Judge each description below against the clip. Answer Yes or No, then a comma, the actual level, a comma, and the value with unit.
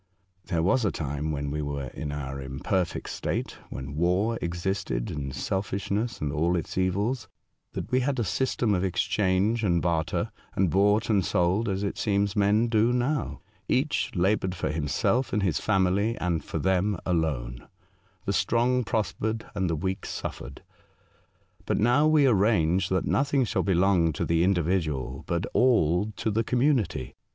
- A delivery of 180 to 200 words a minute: No, average, 165 wpm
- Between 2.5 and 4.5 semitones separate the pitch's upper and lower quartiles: No, average, 4.9 semitones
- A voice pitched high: No, very low, 95 Hz